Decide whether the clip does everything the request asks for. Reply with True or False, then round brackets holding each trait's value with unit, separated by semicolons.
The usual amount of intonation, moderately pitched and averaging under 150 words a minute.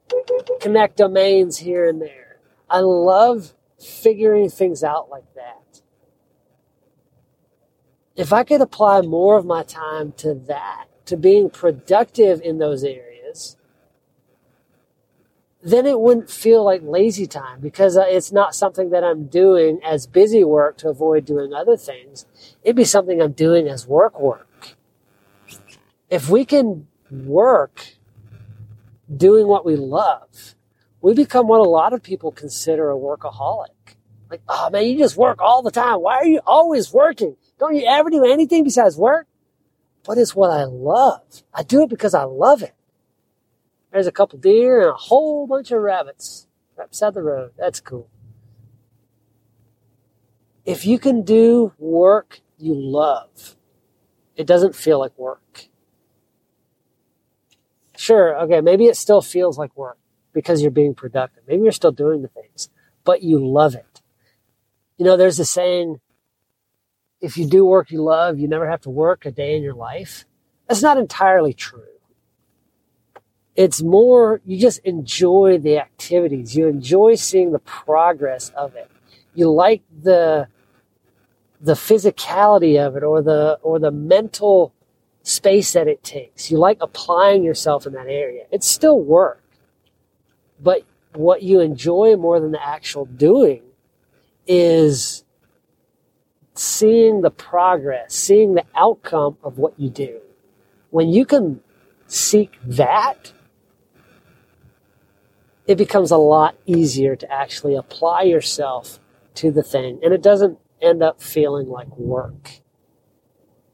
False (6.8 semitones; 165 Hz; 140 wpm)